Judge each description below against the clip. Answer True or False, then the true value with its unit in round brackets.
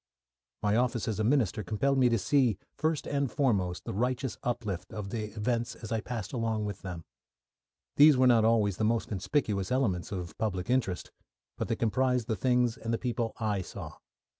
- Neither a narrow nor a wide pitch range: True (3.4 semitones)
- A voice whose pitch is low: True (115 Hz)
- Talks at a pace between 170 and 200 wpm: True (190 wpm)